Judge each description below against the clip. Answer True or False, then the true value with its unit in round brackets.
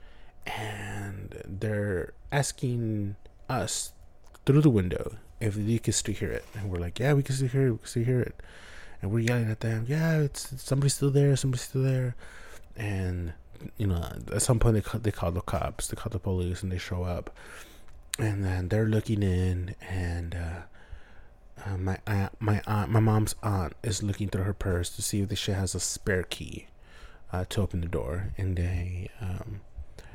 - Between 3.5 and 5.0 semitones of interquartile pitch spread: True (3.8 semitones)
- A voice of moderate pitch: False (105 Hz)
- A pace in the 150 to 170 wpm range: False (195 wpm)